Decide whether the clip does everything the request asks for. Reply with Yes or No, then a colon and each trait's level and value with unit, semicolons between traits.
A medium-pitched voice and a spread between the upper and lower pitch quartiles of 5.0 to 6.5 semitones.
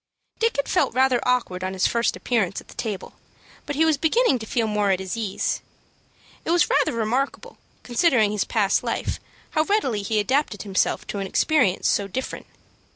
No: high, 230 Hz; wide, 5.5 semitones